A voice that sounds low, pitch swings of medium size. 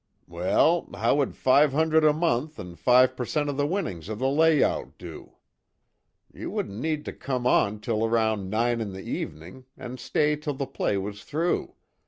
No: low, 130 Hz; wide, 5.9 semitones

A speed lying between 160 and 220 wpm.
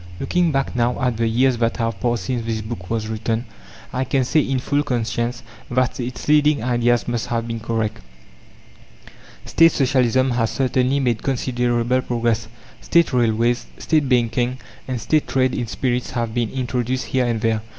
Yes: average, 170 wpm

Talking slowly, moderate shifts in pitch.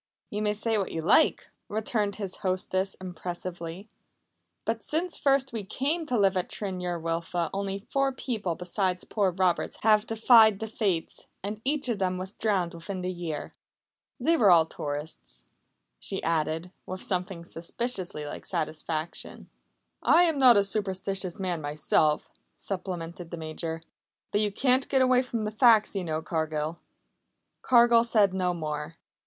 No: average, 155 wpm; average, 4.6 semitones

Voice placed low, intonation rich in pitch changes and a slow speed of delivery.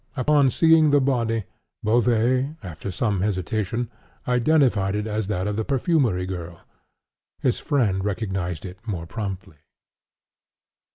No: low, 110 Hz; average, 5.0 semitones; slow, 120 wpm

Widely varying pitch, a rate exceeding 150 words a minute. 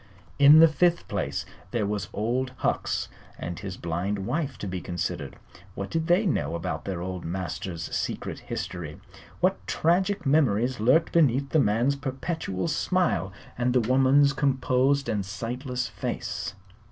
No: wide, 6.7 semitones; average, 145 wpm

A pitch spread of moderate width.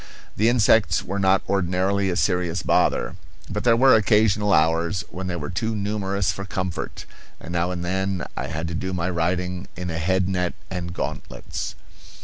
No: narrow, 2.3 semitones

